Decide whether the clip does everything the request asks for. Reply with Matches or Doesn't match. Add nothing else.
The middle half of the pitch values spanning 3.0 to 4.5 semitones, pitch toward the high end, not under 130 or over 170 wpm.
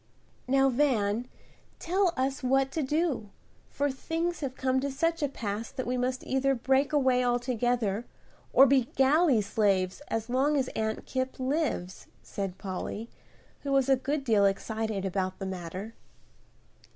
Matches